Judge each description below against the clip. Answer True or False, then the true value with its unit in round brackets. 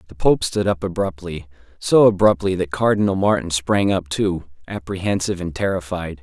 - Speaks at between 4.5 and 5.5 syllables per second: True (5.3 syllables/s)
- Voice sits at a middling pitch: False (90 Hz)